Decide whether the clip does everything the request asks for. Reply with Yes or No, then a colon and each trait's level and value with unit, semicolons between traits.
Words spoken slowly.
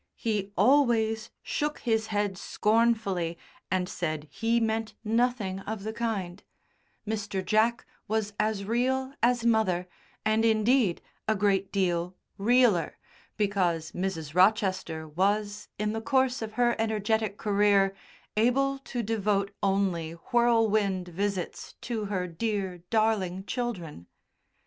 Yes: slow, 120 wpm